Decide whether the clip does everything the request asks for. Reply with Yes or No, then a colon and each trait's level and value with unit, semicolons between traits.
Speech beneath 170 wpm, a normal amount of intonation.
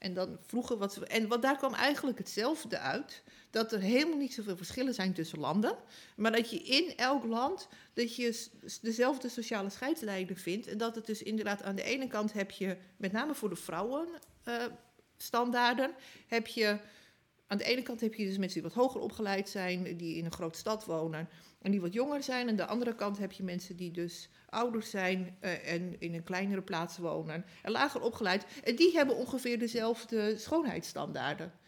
No: average, 190 wpm; average, 4.6 semitones